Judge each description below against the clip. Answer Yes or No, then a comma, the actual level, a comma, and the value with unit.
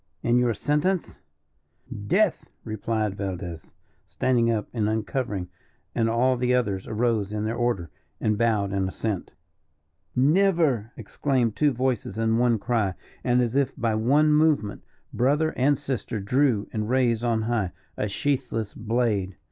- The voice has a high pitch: No, low, 115 Hz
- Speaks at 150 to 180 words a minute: No, average, 140 wpm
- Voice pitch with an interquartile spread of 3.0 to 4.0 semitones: Yes, average, 3.4 semitones